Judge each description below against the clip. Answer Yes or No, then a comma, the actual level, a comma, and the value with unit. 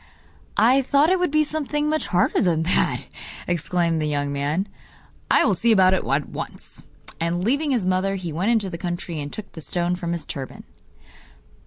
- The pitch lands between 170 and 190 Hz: Yes, medium, 185 Hz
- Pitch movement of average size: No, wide, 6.0 semitones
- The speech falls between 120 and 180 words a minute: No, average, 190 wpm